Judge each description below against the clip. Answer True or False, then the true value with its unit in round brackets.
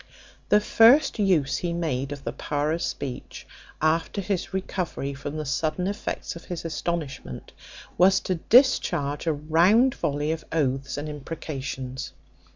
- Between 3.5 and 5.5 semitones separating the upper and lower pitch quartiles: True (4.2 semitones)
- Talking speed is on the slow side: False (145 wpm)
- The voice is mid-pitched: True (160 Hz)